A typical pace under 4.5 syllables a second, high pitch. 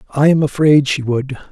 No: 4.2 syllables/s; medium, 140 Hz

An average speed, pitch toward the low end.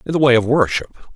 No: fast, 260 wpm; low, 130 Hz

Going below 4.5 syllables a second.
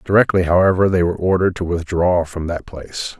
No: 6.2 syllables/s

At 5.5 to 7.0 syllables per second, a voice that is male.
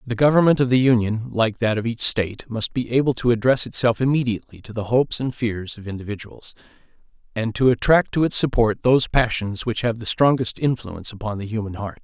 Yes: 5.9 syllables/s; male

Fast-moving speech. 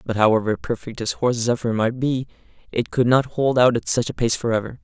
Yes: fast, 225 wpm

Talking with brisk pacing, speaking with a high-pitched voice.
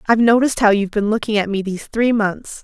Yes: fast, 250 wpm; high, 215 Hz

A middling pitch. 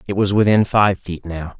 No: very low, 95 Hz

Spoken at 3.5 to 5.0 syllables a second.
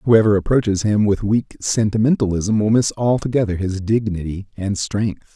Yes: 4.8 syllables/s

